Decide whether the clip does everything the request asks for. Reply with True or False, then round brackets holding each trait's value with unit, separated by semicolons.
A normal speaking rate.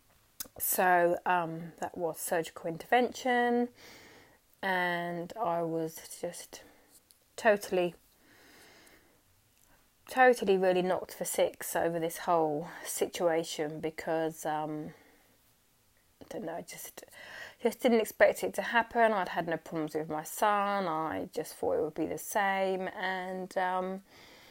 False (120 wpm)